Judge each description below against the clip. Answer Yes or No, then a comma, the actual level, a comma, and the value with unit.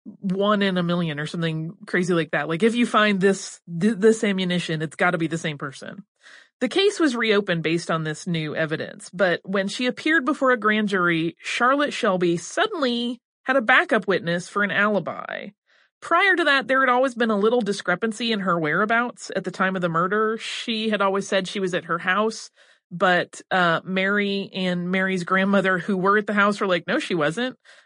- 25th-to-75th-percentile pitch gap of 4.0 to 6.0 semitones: Yes, average, 4.3 semitones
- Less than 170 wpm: No, average, 200 wpm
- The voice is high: Yes, high, 200 Hz